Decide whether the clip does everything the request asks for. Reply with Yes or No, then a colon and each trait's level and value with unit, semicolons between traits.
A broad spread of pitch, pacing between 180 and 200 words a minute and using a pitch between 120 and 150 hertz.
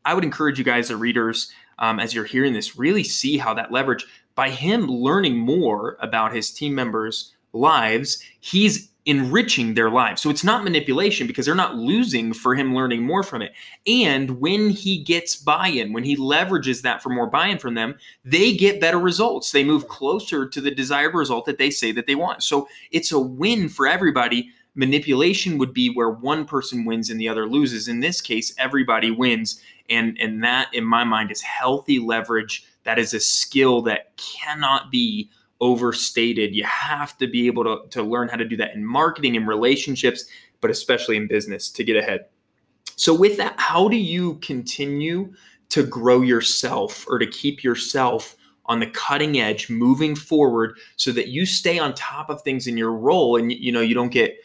Yes: wide, 6.0 semitones; average, 190 wpm; low, 135 Hz